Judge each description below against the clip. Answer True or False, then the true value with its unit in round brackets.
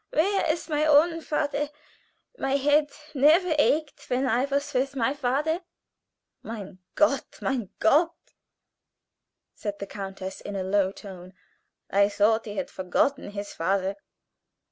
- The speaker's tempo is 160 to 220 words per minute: False (135 wpm)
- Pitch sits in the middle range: False (265 Hz)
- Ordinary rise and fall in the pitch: False (6.6 semitones)